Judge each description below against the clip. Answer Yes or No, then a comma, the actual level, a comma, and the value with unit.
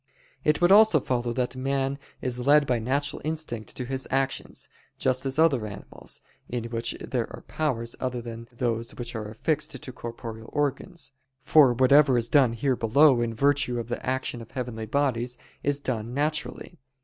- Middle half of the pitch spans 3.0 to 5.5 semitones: Yes, average, 3.3 semitones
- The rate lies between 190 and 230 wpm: No, average, 175 wpm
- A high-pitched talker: No, low, 130 Hz